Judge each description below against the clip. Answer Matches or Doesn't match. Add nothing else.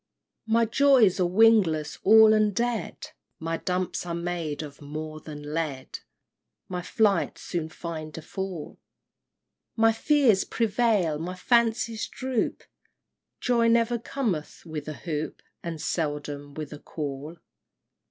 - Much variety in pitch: Matches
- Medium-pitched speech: Matches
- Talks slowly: Matches